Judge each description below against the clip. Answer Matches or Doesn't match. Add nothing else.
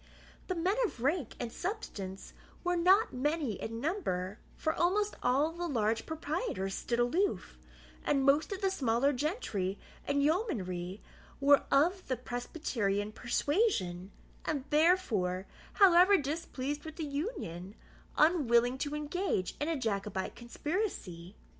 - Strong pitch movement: Matches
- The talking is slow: Matches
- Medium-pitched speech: Doesn't match